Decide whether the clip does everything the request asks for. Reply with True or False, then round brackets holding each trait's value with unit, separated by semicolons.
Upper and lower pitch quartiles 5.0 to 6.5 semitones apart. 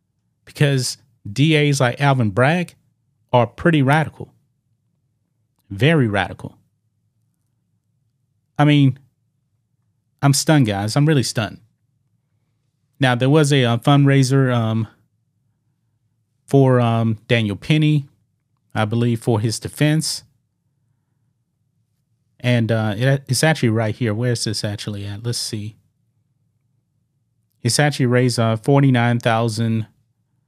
False (2.9 semitones)